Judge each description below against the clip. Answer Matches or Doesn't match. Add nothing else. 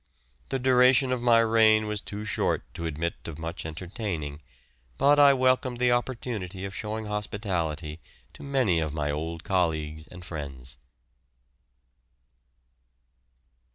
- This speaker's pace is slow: Matches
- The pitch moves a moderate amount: Doesn't match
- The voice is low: Matches